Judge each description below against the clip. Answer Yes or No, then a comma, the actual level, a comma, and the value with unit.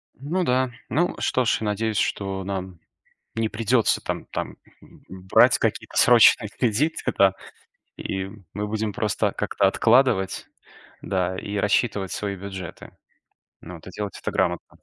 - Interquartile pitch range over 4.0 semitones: No, average, 3.0 semitones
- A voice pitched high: No, low, 105 Hz